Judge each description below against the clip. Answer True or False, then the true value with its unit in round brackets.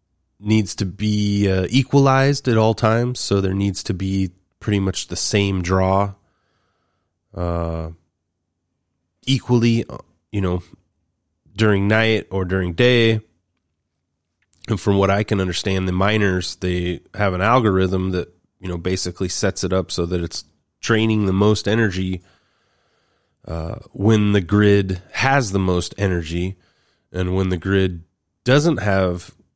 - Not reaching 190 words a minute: True (135 wpm)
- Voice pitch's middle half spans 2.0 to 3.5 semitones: True (2.9 semitones)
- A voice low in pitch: True (95 Hz)